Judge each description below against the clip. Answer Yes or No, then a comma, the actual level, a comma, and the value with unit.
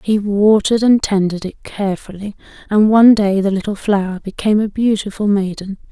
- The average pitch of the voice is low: No, high, 205 Hz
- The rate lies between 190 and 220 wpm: No, average, 160 wpm